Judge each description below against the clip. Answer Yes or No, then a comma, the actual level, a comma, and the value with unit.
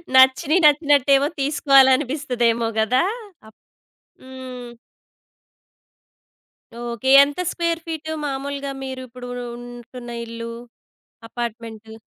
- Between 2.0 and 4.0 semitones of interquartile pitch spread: Yes, average, 2.9 semitones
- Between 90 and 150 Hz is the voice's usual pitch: No, very high, 260 Hz